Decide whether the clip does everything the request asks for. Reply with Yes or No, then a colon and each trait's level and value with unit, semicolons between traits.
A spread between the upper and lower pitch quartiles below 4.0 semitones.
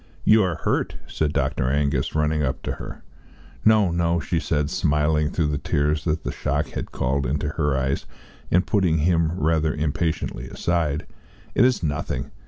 Yes: narrow, 2.5 semitones